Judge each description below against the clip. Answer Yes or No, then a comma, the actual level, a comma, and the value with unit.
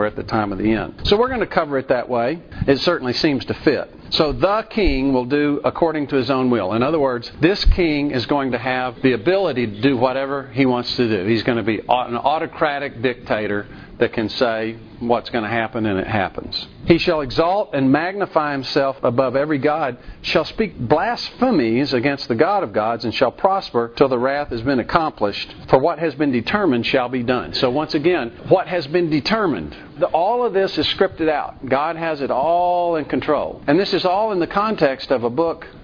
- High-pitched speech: No, low, 135 Hz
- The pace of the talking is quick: Yes, fast, 215 wpm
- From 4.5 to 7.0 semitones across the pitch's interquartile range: Yes, average, 5.3 semitones